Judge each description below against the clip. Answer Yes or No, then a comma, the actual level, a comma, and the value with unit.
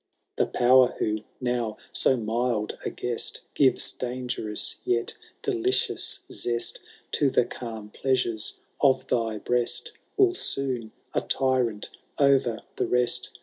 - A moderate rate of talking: No, slow, 120 wpm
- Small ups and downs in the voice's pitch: Yes, narrow, 2.3 semitones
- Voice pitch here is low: Yes, low, 125 Hz